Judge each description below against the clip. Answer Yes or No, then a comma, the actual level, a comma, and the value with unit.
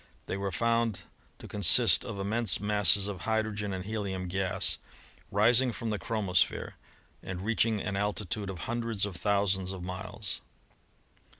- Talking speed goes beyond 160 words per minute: No, average, 140 wpm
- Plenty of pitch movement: No, narrow, 2.5 semitones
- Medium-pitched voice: No, low, 100 Hz